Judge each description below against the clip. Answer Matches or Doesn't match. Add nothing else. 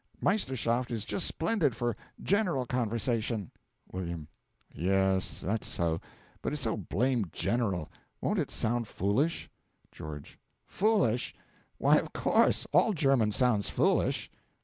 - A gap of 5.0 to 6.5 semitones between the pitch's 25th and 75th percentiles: Matches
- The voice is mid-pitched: Doesn't match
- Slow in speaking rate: Matches